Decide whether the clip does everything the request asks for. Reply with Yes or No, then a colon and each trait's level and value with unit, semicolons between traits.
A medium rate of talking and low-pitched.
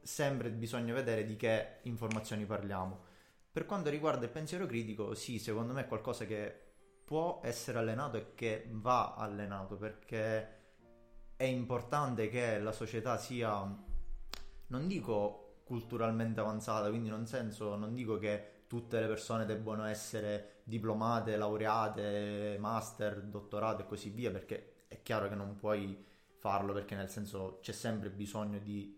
Yes: average, 145 wpm; low, 110 Hz